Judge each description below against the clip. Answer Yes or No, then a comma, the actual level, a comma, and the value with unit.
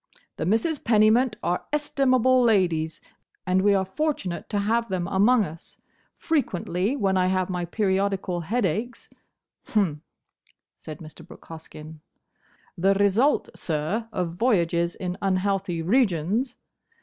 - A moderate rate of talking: No, slow, 125 wpm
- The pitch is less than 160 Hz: No, high, 195 Hz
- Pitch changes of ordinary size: Yes, average, 4.7 semitones